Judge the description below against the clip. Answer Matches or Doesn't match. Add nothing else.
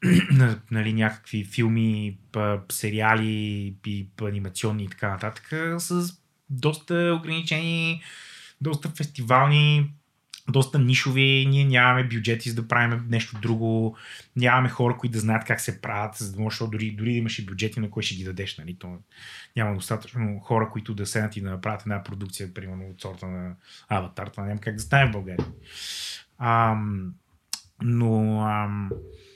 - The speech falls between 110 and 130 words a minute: Doesn't match